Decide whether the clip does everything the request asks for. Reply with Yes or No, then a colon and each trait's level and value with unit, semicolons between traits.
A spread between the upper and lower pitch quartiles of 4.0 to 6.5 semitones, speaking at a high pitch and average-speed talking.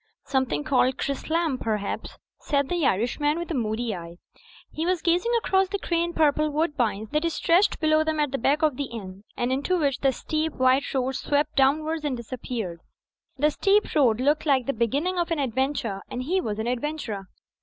Yes: average, 4.4 semitones; very high, 280 Hz; average, 190 wpm